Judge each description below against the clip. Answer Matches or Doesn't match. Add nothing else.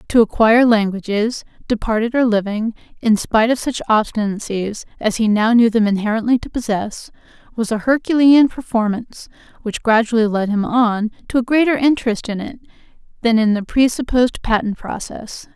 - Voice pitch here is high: Matches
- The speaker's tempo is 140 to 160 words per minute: Matches